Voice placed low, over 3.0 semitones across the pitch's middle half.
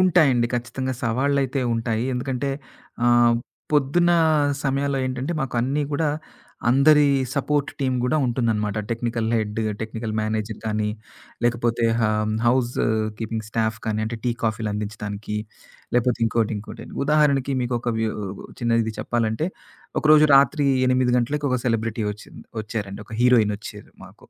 Yes: low, 120 Hz; average, 3.5 semitones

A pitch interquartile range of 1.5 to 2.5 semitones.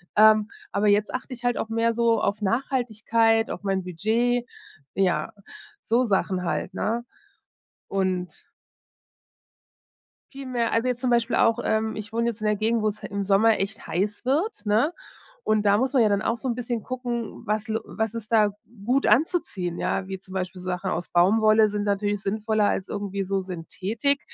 No: average, 2.9 semitones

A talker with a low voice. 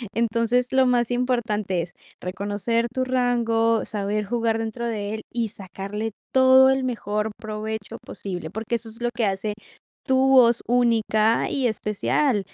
No: high, 225 Hz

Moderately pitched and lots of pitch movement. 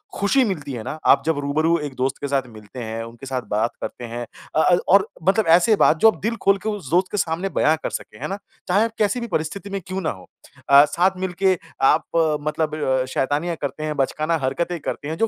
Yes: medium, 160 Hz; wide, 5.9 semitones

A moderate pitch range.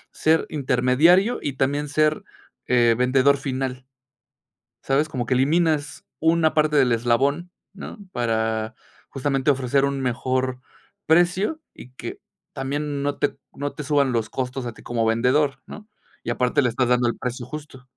Yes: average, 3.1 semitones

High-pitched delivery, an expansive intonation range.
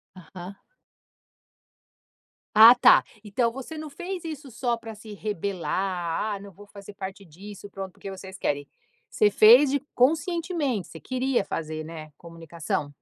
Yes: high, 205 Hz; wide, 5.7 semitones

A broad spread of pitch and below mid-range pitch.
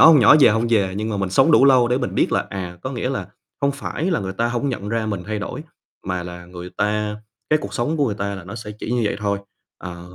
No: average, 4.5 semitones; low, 105 Hz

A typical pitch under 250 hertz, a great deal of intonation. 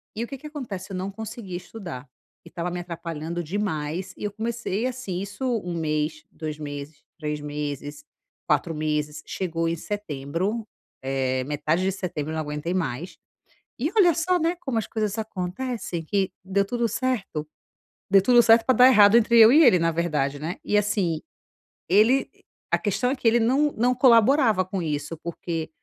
Yes: medium, 185 Hz; wide, 6.5 semitones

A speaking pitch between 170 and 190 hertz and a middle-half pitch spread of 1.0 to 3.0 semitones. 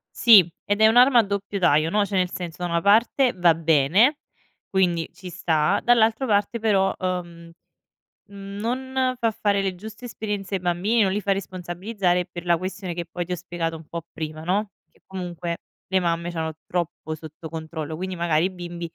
No: medium, 185 Hz; average, 3.4 semitones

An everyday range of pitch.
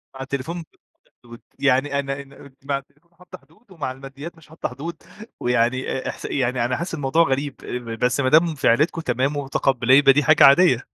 Yes: average, 3.2 semitones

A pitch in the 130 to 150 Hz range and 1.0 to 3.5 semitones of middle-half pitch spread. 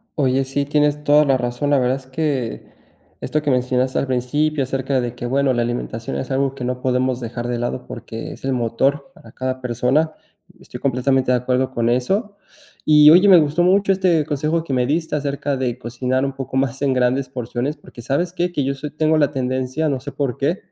Yes: low, 135 Hz; average, 2.8 semitones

